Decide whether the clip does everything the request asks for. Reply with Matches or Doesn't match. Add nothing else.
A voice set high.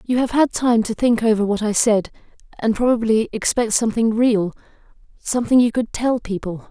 Matches